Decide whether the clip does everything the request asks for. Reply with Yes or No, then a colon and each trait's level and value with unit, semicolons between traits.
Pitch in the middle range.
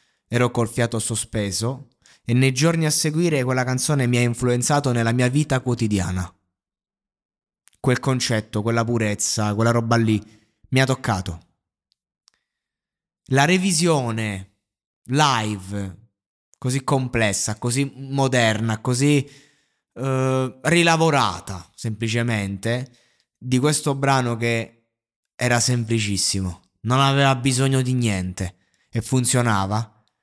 No: low, 120 Hz